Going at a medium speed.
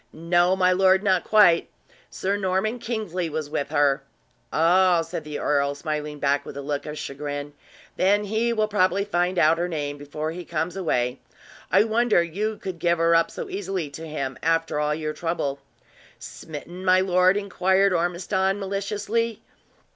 Yes: average, 165 wpm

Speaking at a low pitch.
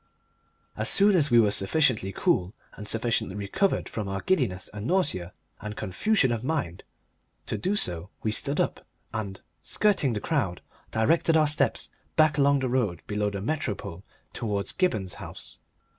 Yes: low, 110 Hz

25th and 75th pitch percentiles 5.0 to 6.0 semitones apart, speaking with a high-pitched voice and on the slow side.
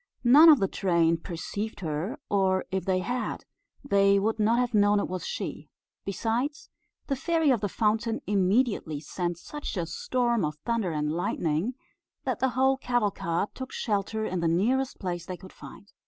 No: average, 5.3 semitones; high, 205 Hz; average, 170 wpm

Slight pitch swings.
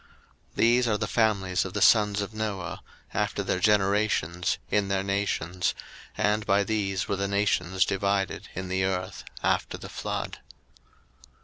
Yes: narrow, 1.8 semitones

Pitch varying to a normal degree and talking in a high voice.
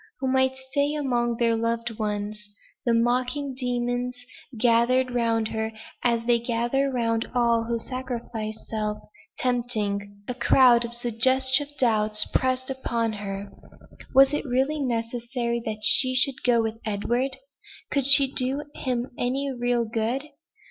No: narrow, 2.2 semitones; high, 240 Hz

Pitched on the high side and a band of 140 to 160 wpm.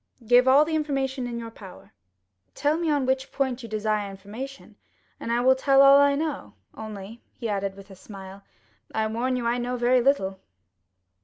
No: high, 245 Hz; average, 185 wpm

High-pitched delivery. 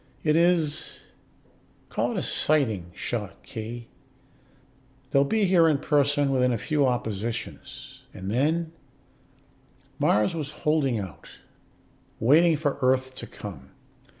No: low, 135 Hz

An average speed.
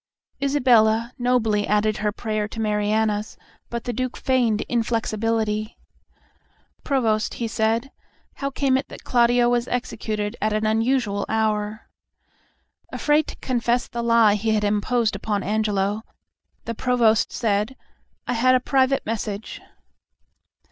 No: slow, 125 wpm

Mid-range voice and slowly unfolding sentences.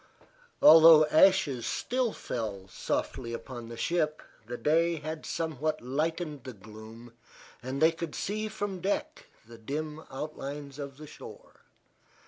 Yes: medium, 150 Hz; slow, 130 wpm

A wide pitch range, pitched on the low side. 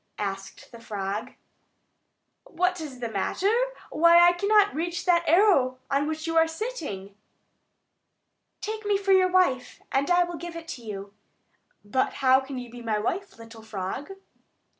No: wide, 7.6 semitones; very high, 305 Hz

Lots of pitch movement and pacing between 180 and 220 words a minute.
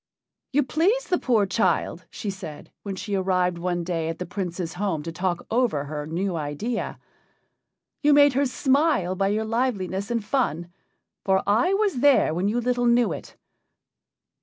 No: wide, 6.0 semitones; average, 165 wpm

